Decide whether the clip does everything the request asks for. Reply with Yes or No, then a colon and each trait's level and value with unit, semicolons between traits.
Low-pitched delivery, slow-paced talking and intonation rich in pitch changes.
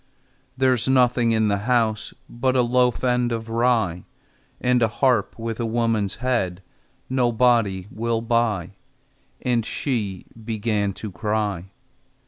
No: low, 115 Hz; slow, 125 wpm; average, 2.7 semitones